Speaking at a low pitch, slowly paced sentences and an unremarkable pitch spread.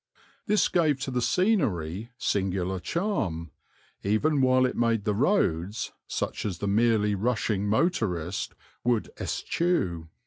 No: low, 110 Hz; slow, 125 wpm; wide, 5.9 semitones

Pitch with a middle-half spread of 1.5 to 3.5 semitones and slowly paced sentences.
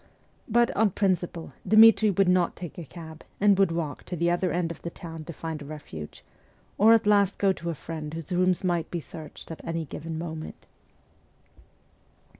No: average, 3.0 semitones; average, 190 wpm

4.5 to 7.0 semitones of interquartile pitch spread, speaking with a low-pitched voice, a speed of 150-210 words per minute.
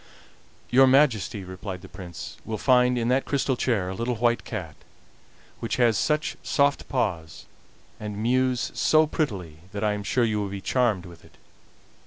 Yes: average, 4.8 semitones; low, 115 Hz; average, 170 wpm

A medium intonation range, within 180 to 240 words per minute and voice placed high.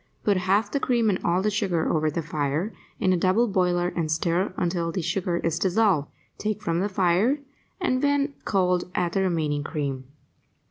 No: average, 3.6 semitones; average, 185 wpm; medium, 180 Hz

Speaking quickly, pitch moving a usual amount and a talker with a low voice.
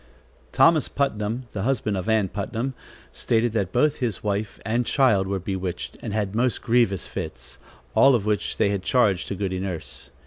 No: average, 170 wpm; average, 3.8 semitones; low, 105 Hz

